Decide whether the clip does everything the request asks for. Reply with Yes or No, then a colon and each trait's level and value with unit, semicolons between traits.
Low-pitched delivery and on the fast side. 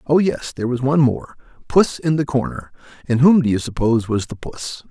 Yes: low, 130 Hz; fast, 220 wpm